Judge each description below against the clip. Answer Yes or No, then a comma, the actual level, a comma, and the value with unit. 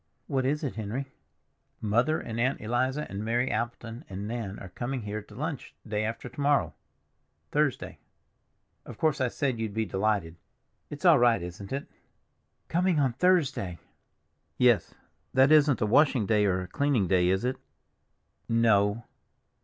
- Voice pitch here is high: No, low, 120 Hz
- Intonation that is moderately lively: Yes, average, 4.7 semitones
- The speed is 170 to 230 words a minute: No, average, 155 wpm